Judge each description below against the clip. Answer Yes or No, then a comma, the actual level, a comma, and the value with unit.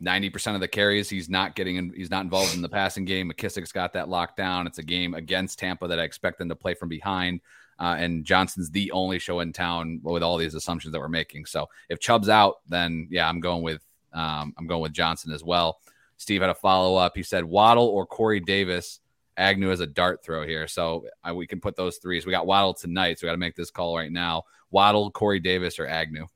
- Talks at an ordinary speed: No, fast, 245 wpm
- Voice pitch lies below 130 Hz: Yes, very low, 90 Hz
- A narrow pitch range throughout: Yes, narrow, 2.1 semitones